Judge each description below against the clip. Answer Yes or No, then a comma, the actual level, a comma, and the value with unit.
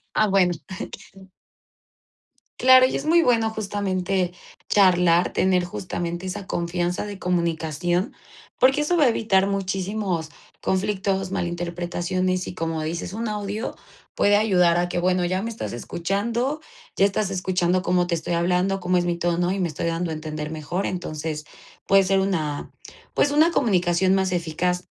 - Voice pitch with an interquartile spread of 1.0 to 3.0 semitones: Yes, narrow, 2.4 semitones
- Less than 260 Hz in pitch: Yes, medium, 185 Hz